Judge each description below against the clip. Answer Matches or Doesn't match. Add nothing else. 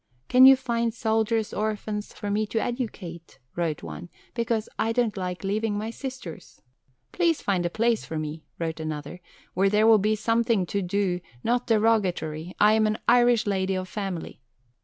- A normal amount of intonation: Matches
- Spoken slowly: Doesn't match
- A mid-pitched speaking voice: Doesn't match